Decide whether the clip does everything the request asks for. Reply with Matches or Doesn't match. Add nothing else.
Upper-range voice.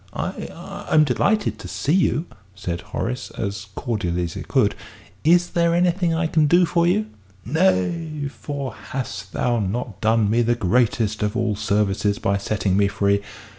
Doesn't match